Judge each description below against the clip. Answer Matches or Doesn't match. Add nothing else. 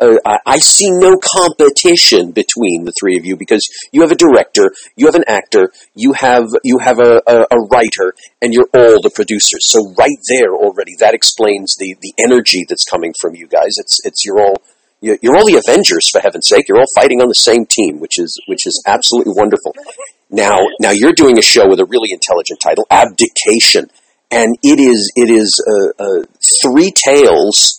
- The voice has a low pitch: Doesn't match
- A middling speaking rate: Matches